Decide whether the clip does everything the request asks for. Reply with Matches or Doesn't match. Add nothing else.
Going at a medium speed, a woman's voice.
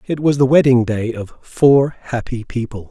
Doesn't match